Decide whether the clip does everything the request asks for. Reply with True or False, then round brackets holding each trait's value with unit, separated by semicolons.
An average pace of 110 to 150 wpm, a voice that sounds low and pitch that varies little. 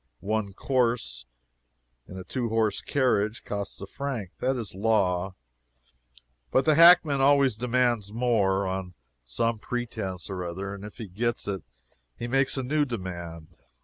False (145 wpm; 110 Hz; 4.7 semitones)